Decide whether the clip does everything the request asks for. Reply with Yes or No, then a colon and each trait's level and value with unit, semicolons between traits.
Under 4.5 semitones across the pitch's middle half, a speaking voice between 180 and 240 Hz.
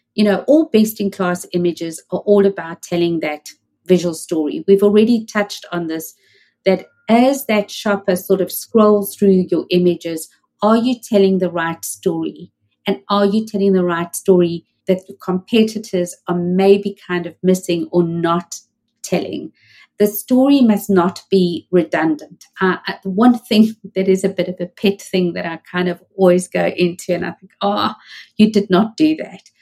Yes: average, 2.8 semitones; medium, 185 Hz